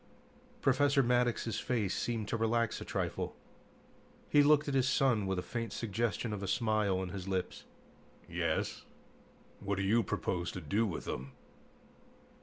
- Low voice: Yes, low, 110 Hz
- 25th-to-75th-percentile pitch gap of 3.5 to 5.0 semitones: Yes, average, 4.0 semitones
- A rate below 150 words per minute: No, average, 155 wpm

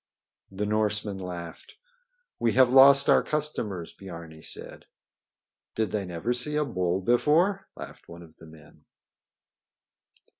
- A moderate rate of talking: No, slow, 125 wpm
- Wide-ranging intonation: Yes, wide, 7.0 semitones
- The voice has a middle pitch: No, low, 105 Hz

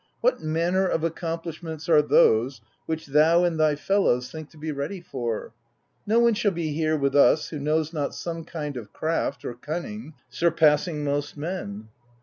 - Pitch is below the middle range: No, medium, 155 Hz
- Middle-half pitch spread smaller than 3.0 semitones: Yes, narrow, 2.6 semitones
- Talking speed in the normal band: Yes, average, 170 wpm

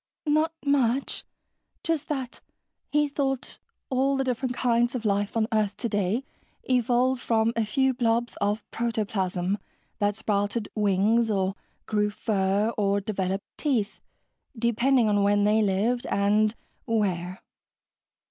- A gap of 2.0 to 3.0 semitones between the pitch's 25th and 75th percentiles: No, average, 3.5 semitones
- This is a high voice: Yes, high, 220 Hz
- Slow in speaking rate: Yes, slow, 125 wpm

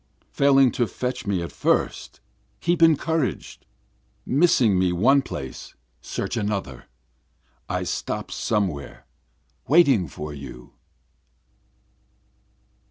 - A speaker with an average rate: No, slow, 95 wpm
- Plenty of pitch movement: Yes, wide, 8.1 semitones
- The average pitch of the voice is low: Yes, low, 110 Hz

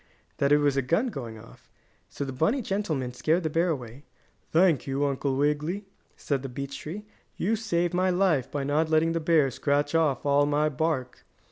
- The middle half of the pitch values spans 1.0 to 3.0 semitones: No, average, 3.6 semitones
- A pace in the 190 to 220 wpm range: Yes, average, 195 wpm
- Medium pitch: Yes, medium, 150 Hz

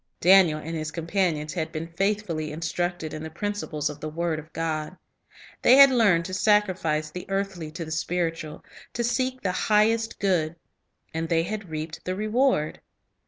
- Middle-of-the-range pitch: Yes, medium, 170 Hz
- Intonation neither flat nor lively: Yes, average, 4.2 semitones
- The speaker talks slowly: No, average, 165 wpm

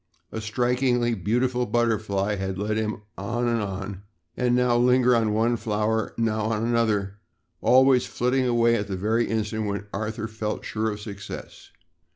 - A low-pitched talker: Yes, low, 110 Hz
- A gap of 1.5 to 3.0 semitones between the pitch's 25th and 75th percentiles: Yes, narrow, 2.4 semitones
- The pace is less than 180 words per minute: Yes, average, 155 wpm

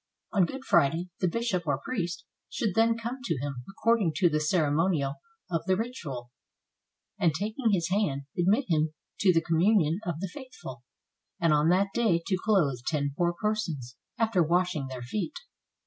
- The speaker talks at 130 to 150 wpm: No, average, 165 wpm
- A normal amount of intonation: No, wide, 5.7 semitones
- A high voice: No, medium, 175 Hz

